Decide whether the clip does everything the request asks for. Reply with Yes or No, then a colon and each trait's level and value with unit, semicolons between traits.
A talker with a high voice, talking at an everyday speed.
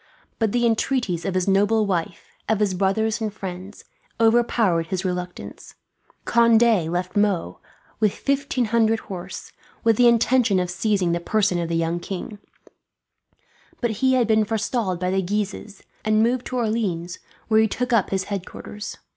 Yes: high, 210 Hz; average, 160 wpm